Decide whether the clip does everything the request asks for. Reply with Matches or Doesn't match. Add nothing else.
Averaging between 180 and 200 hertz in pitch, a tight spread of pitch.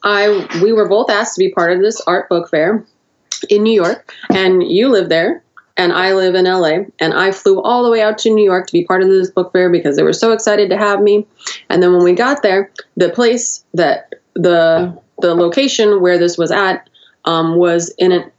Doesn't match